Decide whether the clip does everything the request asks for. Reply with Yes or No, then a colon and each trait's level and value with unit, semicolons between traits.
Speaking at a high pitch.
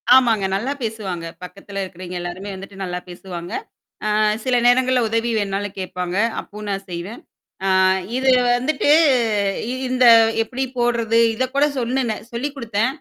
Yes: high, 220 Hz